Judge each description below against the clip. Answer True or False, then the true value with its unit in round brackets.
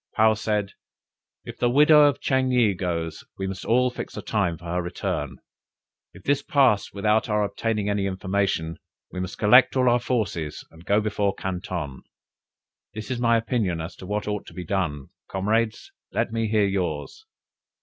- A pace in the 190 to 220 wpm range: False (170 wpm)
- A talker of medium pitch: False (105 Hz)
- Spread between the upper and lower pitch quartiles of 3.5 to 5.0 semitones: True (3.8 semitones)